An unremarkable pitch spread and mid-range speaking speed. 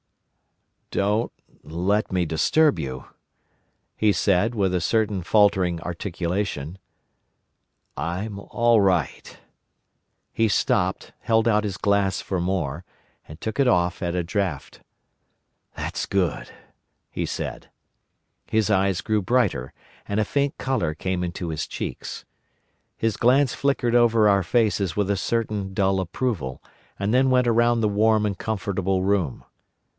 No: average, 3.8 semitones; slow, 130 wpm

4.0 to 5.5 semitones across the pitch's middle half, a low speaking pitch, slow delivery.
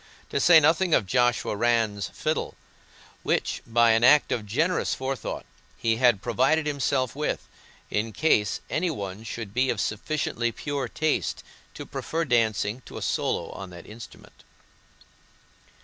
No: average, 4.9 semitones; low, 120 Hz; average, 145 wpm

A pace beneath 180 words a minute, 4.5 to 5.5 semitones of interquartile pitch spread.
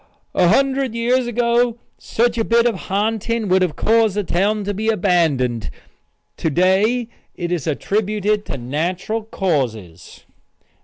Yes: average, 140 wpm; average, 4.8 semitones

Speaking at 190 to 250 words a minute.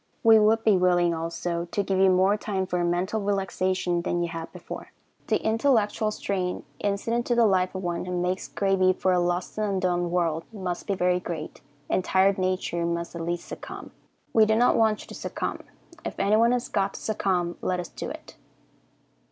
Yes: average, 195 wpm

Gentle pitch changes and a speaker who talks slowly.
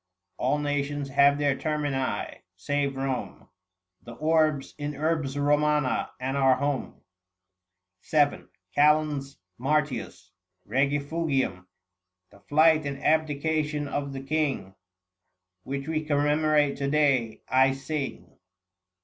Yes: narrow, 1.8 semitones; slow, 105 wpm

